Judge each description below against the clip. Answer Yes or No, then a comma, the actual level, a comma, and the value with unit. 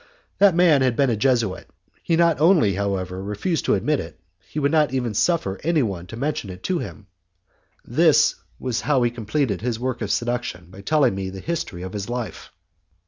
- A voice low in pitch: Yes, low, 120 Hz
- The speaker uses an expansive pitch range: Yes, wide, 7.1 semitones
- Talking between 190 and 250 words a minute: Yes, average, 195 wpm